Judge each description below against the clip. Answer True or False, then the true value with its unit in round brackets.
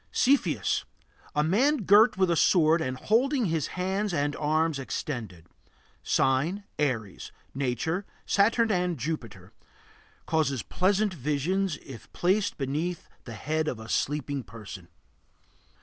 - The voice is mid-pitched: True (155 Hz)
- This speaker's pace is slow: True (120 wpm)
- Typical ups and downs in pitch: False (6.4 semitones)